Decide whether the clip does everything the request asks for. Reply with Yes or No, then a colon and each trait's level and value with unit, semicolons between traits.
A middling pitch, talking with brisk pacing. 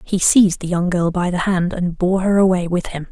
Yes: medium, 180 Hz; fast, 270 wpm